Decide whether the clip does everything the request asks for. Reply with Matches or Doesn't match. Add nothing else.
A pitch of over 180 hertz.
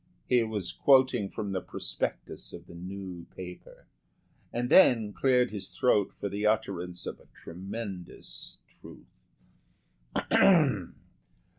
Doesn't match